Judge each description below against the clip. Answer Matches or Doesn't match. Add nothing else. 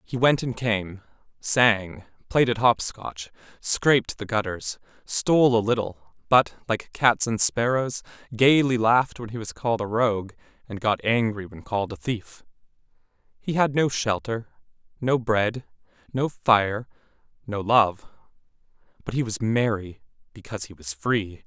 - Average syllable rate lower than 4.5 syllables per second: Matches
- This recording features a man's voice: Matches